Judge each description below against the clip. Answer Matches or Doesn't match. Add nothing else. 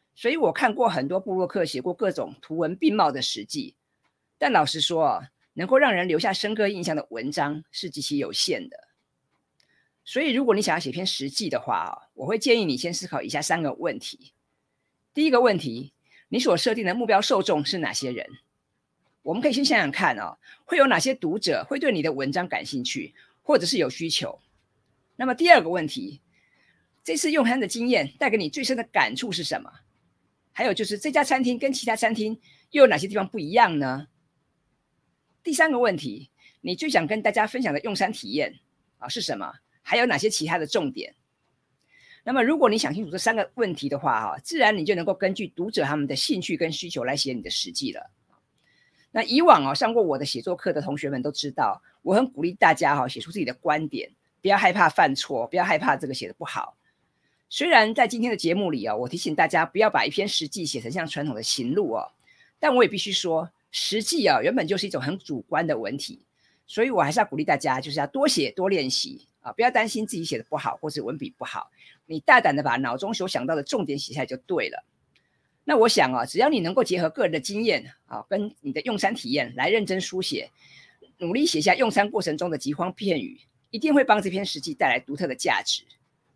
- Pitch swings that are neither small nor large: Doesn't match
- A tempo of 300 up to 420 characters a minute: Matches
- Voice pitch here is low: Doesn't match